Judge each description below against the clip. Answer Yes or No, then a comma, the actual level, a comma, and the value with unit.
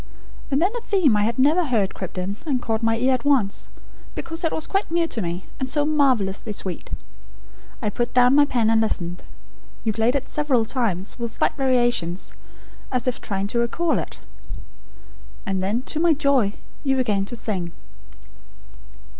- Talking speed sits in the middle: Yes, average, 180 wpm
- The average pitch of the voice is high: Yes, high, 240 Hz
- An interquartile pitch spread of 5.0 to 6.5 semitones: Yes, wide, 5.4 semitones